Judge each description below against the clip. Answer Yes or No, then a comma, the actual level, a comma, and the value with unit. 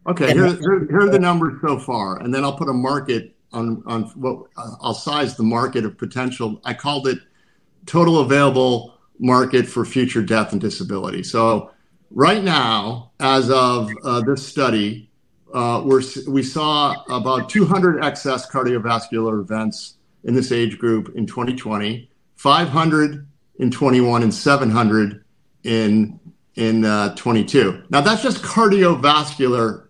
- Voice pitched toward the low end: Yes, low, 130 Hz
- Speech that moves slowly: No, average, 155 wpm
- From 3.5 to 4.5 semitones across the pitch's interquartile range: Yes, average, 4.1 semitones